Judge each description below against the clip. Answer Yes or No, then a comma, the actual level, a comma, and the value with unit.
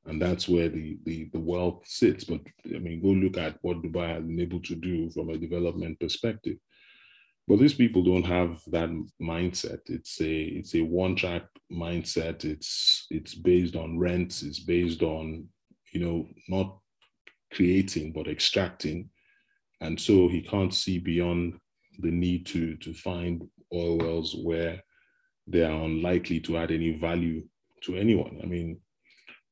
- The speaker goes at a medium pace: Yes, average, 155 wpm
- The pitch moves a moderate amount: No, narrow, 1.4 semitones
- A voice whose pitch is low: Yes, very low, 85 Hz